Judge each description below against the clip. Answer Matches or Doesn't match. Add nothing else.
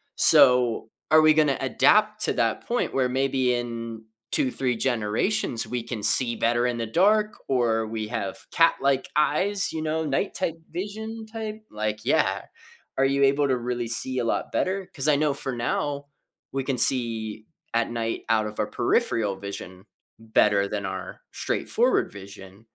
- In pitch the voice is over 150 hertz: Doesn't match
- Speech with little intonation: Doesn't match